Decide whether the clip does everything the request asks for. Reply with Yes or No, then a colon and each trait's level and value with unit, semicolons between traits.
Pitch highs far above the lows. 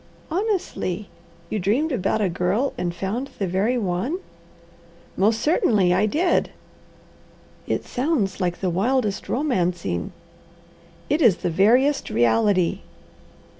Yes: wide, 6.5 semitones